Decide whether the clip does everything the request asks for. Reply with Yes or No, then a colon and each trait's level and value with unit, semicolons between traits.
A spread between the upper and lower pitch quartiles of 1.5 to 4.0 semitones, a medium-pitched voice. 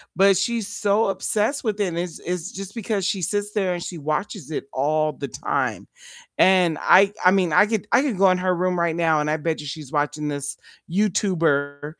No: average, 4.5 semitones; medium, 180 Hz